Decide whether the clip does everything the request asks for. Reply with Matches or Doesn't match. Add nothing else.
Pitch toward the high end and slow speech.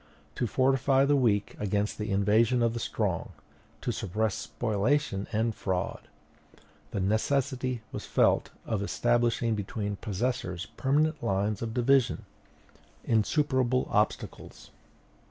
Doesn't match